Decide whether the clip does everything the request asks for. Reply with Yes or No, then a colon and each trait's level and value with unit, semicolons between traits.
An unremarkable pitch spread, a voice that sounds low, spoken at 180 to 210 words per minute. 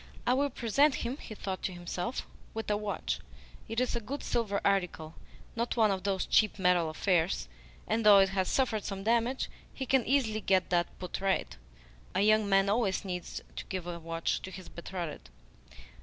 No: average, 3.8 semitones; high, 200 Hz; average, 185 wpm